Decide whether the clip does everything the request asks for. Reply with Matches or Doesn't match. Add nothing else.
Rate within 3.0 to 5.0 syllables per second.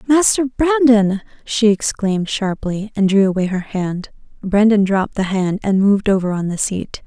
Matches